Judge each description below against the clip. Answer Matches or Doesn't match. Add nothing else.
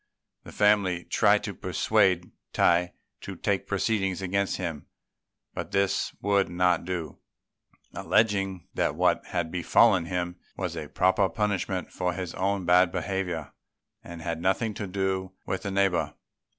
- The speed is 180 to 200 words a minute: Doesn't match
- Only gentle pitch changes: Matches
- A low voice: Matches